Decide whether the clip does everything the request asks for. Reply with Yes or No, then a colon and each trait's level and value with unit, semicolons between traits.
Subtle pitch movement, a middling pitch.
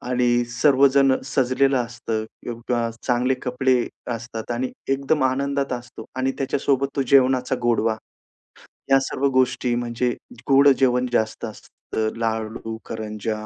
No: narrow, 2.3 semitones; low, 125 Hz